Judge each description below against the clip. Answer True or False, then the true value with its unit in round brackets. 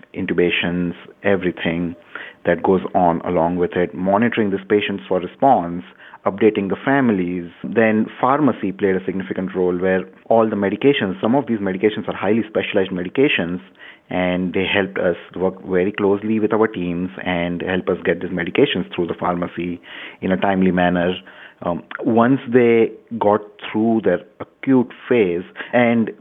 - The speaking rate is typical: True (150 wpm)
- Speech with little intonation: False (3.4 semitones)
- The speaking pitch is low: True (95 Hz)